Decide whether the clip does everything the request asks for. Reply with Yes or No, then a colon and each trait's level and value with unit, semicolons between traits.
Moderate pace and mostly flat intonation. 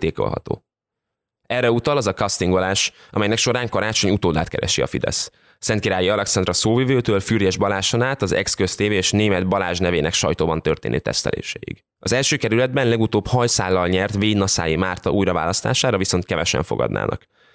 No: average, 135 wpm; average, 3.9 semitones